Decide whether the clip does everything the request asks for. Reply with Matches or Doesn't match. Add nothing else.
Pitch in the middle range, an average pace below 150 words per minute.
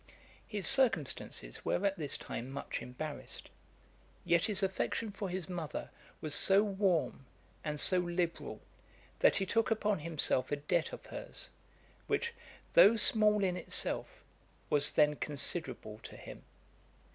Matches